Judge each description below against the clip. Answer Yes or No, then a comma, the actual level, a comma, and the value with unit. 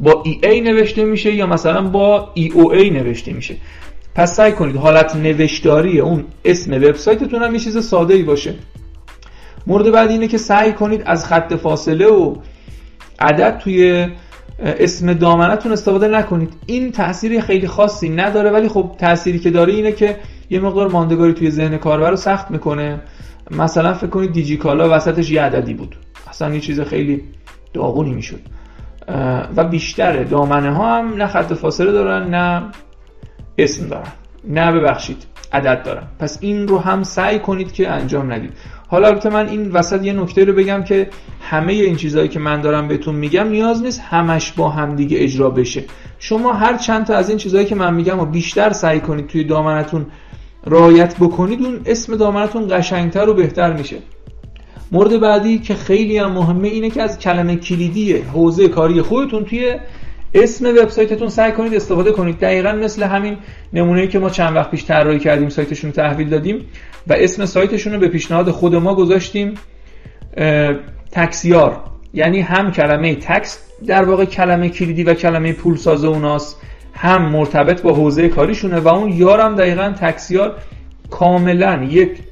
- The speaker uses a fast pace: Yes, fast, 165 wpm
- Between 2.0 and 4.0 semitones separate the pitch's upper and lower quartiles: No, average, 4.6 semitones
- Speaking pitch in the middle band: Yes, medium, 175 Hz